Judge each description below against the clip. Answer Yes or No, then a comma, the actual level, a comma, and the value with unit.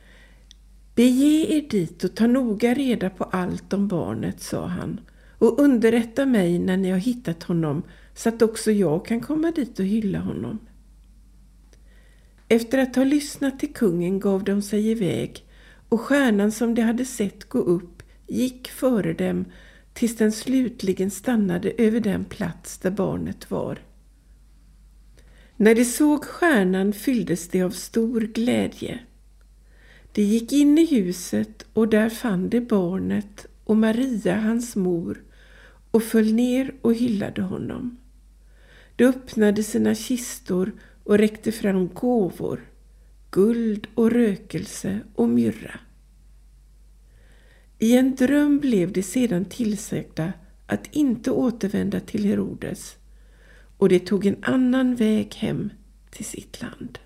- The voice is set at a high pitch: Yes, high, 215 Hz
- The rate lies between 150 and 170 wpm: No, average, 135 wpm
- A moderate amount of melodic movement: Yes, average, 4.7 semitones